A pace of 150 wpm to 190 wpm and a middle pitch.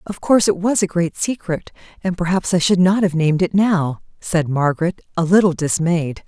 No: average, 200 wpm; medium, 175 Hz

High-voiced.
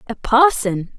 Yes: high, 205 Hz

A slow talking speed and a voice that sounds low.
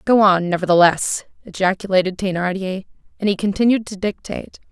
No: slow, 125 wpm; high, 195 Hz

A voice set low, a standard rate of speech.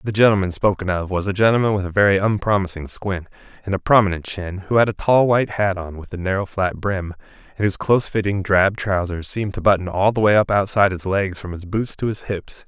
No: low, 100 Hz; fast, 235 wpm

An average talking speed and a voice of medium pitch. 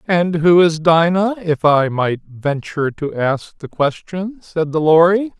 Yes: average, 165 wpm; medium, 165 Hz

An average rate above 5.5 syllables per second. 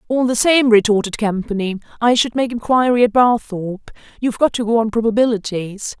Yes: 5.7 syllables/s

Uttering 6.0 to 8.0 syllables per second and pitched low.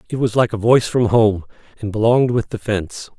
Yes: 6.2 syllables/s; low, 110 Hz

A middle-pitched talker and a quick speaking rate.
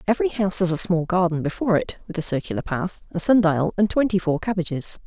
Yes: medium, 180 Hz; fast, 225 wpm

